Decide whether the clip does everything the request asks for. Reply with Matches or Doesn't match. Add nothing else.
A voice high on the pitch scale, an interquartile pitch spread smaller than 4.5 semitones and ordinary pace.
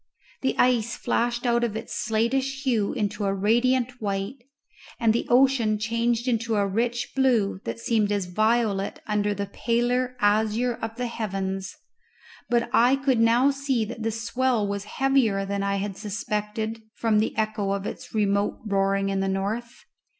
Matches